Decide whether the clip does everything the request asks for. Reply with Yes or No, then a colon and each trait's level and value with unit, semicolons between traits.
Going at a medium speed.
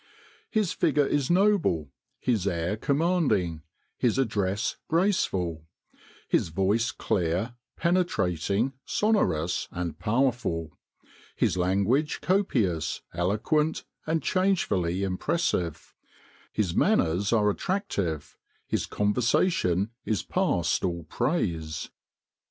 No: slow, 90 wpm